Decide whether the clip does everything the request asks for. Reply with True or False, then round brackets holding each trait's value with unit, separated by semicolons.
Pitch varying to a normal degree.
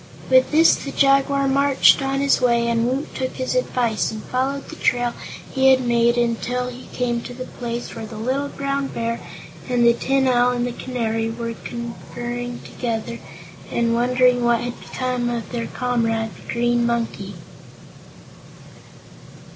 False (1.7 semitones)